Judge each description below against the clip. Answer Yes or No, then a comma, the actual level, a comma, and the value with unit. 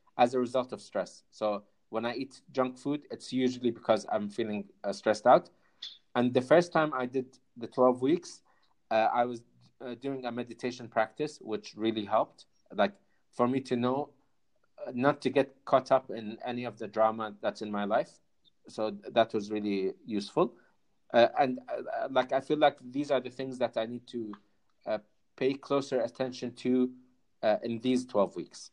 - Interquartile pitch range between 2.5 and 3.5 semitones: Yes, average, 3.0 semitones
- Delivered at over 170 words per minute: Yes, average, 190 wpm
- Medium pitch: No, low, 125 Hz